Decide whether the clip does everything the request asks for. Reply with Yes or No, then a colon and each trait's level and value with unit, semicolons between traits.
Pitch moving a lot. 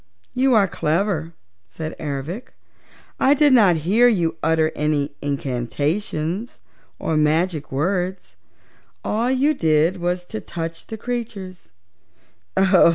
Yes: wide, 5.7 semitones